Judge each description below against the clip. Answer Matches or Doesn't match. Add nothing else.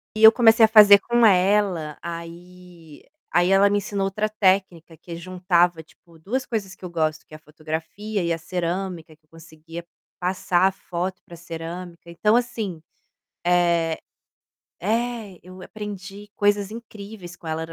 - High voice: Doesn't match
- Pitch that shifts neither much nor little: Matches